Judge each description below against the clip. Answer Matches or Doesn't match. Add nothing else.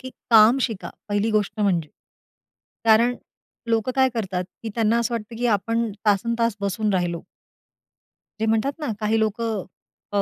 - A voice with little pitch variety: Matches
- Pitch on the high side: Matches